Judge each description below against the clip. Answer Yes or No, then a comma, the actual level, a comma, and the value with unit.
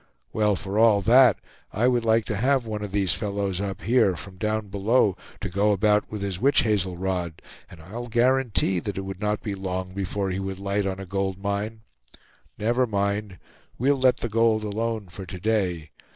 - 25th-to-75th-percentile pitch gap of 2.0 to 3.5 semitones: Yes, narrow, 2.6 semitones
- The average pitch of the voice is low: Yes, low, 100 Hz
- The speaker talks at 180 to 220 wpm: Yes, average, 195 wpm